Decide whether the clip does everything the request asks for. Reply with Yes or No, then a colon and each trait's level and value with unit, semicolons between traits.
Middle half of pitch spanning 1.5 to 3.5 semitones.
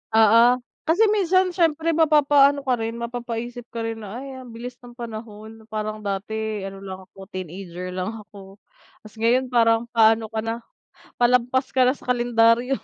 Yes: average, 2.9 semitones